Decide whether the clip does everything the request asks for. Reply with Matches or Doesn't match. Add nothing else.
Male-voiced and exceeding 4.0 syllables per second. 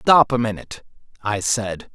Matches